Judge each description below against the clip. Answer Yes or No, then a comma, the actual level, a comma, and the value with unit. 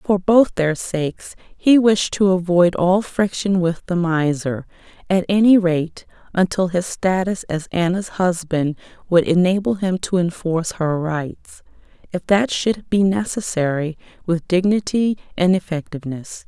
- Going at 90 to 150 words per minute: Yes, average, 140 wpm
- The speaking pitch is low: No, medium, 180 Hz